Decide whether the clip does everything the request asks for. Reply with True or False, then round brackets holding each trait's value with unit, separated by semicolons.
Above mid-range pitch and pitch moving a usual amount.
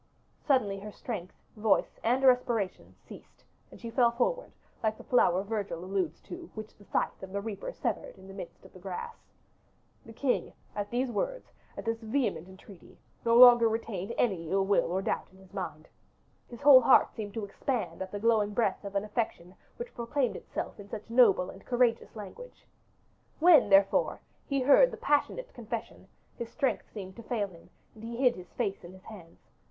True (220 Hz; 4.1 semitones)